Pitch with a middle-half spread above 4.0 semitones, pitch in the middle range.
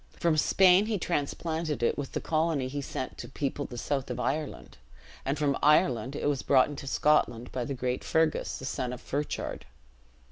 No: average, 3.1 semitones; medium, 145 Hz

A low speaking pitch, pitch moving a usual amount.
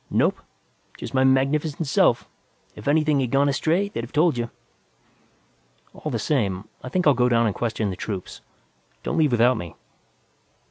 Yes: low, 130 Hz; average, 4.5 semitones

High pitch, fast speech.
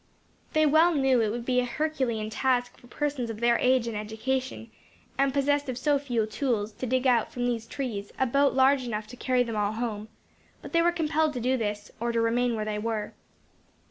Yes: high, 245 Hz; fast, 215 wpm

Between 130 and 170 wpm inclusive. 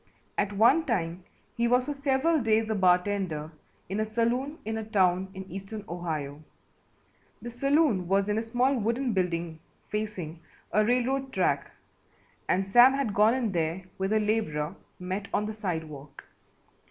Yes: average, 155 wpm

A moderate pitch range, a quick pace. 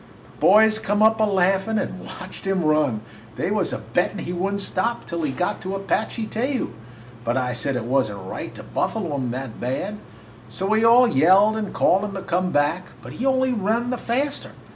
No: wide, 6.7 semitones; fast, 210 wpm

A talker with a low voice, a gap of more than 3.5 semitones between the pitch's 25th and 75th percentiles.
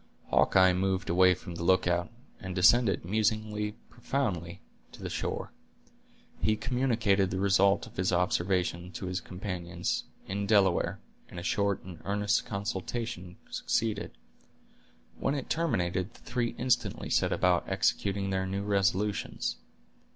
No: very low, 95 Hz; average, 2.8 semitones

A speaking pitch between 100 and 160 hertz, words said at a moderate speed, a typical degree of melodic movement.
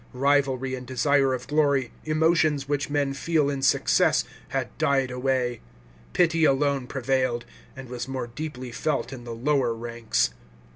No: low, 135 Hz; average, 145 wpm; narrow, 2.3 semitones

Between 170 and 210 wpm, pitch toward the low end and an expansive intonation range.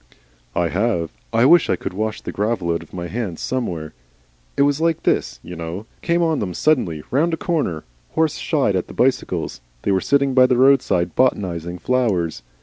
Yes: average, 190 wpm; low, 110 Hz; wide, 8.0 semitones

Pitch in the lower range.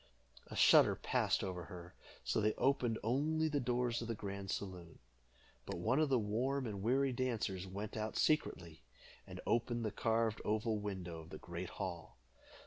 Yes: low, 110 Hz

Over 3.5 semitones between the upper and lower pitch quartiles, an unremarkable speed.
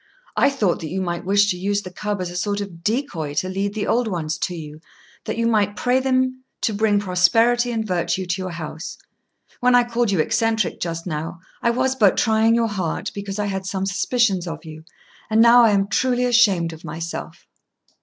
No: average, 4.7 semitones; fast, 210 wpm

